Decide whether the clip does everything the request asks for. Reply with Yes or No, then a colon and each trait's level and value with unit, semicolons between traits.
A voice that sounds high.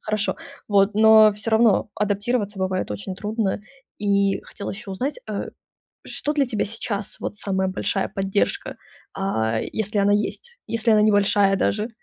Yes: high, 205 Hz